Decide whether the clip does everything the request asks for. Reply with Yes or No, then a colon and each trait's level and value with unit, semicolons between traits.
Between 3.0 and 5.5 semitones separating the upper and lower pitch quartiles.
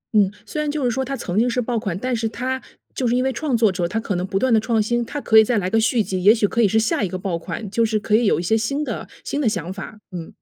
Yes: average, 3.7 semitones